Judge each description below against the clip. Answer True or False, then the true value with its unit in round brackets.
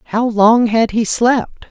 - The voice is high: True (230 Hz)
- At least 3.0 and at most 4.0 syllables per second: True (3.5 syllables/s)